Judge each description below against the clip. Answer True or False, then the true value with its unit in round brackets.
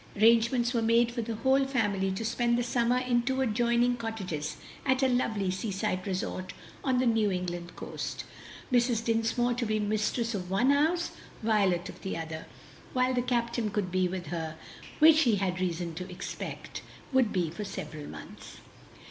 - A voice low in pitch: False (225 Hz)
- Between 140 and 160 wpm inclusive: False (175 wpm)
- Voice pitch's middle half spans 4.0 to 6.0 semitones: True (4.7 semitones)